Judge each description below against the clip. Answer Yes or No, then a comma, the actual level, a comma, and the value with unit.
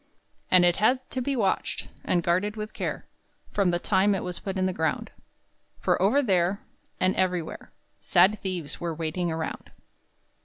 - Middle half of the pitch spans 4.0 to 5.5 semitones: No, average, 2.9 semitones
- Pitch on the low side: No, medium, 185 Hz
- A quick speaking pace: No, average, 165 wpm